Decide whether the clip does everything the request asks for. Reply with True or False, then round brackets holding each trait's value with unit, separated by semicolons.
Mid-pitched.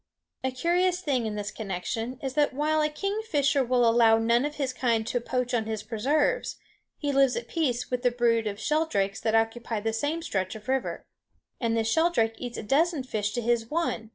False (245 Hz)